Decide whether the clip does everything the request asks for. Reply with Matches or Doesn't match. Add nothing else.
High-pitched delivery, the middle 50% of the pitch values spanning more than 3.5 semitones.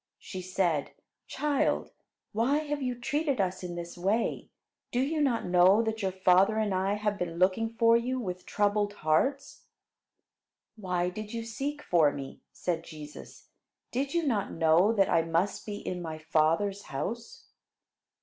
Matches